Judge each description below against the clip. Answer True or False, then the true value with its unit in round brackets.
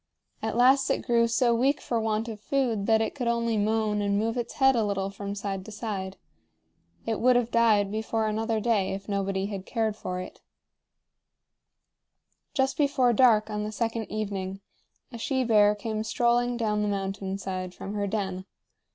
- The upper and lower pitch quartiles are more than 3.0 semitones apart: False (2.7 semitones)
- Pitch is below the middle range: False (220 Hz)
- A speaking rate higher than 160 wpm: True (180 wpm)